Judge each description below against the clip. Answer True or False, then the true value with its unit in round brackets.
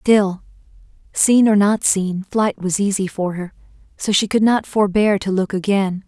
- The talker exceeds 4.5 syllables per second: False (4.3 syllables/s)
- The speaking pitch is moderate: False (200 Hz)